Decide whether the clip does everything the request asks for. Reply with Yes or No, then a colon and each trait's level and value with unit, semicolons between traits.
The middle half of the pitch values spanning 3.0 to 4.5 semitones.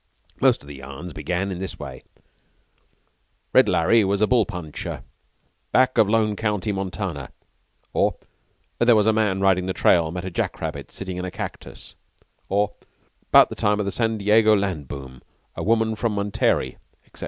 Yes: average, 3.5 semitones